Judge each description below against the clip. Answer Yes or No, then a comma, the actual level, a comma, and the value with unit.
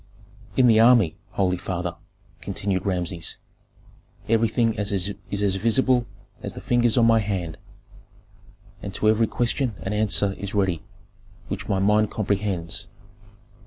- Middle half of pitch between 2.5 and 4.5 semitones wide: Yes, average, 3.2 semitones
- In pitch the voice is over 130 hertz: No, low, 105 Hz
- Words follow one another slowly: Yes, slow, 125 wpm